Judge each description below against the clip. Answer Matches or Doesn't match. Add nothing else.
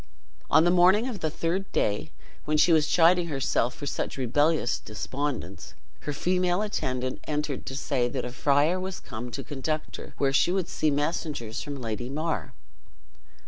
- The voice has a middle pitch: Matches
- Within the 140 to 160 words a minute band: Doesn't match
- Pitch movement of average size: Matches